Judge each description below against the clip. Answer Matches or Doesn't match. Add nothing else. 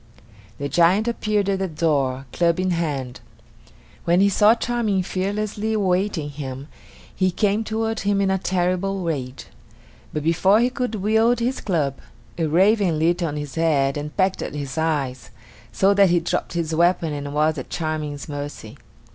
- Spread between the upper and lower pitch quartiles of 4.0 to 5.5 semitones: Matches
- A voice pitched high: Doesn't match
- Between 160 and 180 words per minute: Matches